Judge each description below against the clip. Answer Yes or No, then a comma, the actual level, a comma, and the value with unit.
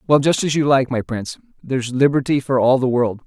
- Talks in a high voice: No, low, 135 Hz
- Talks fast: Yes, fast, 240 wpm